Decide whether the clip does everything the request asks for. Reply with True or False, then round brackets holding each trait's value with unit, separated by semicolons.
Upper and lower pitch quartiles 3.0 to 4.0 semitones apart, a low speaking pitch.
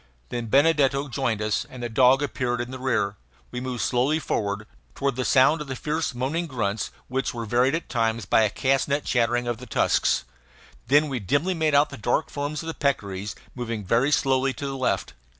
True (3.3 semitones; 130 Hz)